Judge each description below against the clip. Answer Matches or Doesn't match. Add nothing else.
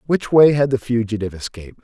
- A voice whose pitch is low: Matches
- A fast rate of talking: Doesn't match